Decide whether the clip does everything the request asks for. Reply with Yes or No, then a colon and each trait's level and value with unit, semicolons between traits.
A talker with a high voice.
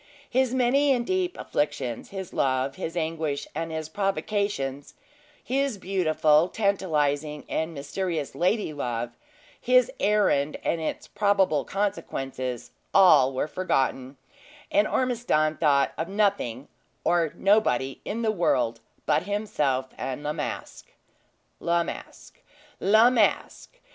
No: medium, 165 Hz